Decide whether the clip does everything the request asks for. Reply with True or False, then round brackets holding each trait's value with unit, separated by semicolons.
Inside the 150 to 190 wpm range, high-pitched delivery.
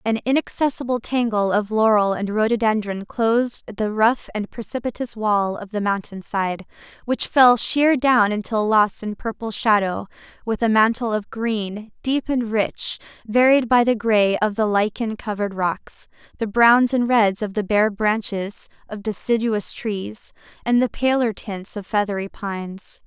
True (160 wpm; 220 Hz)